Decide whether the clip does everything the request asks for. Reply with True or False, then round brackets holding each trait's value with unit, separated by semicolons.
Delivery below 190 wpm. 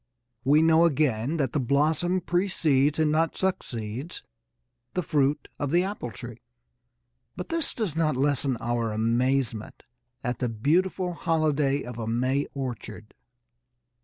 True (135 wpm)